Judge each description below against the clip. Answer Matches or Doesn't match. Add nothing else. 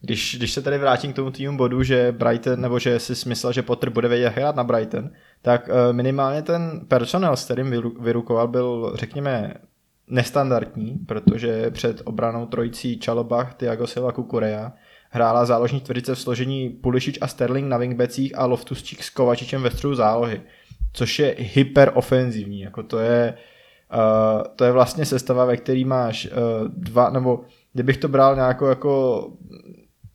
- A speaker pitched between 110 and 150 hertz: Matches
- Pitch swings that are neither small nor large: Doesn't match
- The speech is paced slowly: Doesn't match